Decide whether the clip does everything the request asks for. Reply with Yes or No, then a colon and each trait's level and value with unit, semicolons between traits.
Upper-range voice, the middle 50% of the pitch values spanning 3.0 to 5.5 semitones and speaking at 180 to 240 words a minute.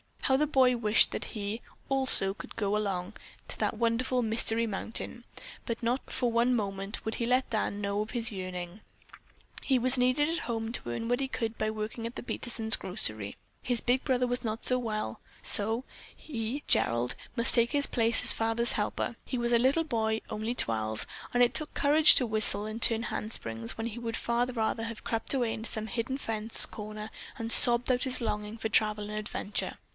No: high, 230 Hz; narrow, 2.5 semitones; average, 195 wpm